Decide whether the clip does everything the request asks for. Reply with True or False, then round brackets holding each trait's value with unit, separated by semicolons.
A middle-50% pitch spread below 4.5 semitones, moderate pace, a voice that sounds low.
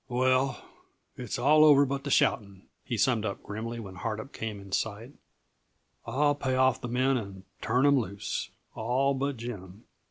True (4.0 semitones; 165 wpm; 120 Hz)